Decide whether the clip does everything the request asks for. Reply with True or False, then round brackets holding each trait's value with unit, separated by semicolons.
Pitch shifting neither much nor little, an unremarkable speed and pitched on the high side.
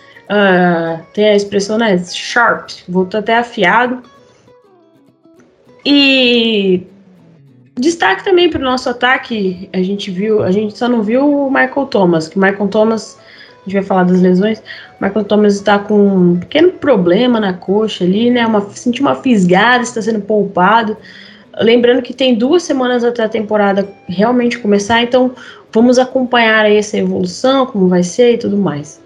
True (4.3 semitones; 155 wpm; 215 Hz)